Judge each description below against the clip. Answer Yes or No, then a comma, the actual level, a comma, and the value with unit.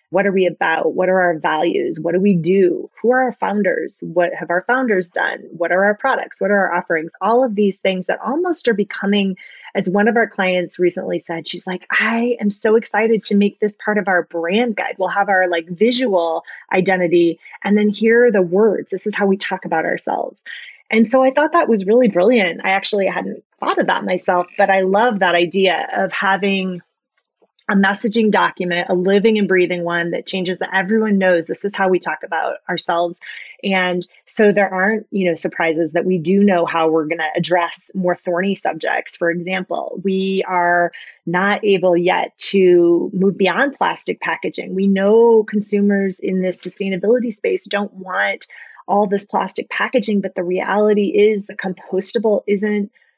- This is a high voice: Yes, high, 195 Hz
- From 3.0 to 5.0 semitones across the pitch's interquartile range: No, narrow, 2.6 semitones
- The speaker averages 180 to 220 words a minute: Yes, average, 190 wpm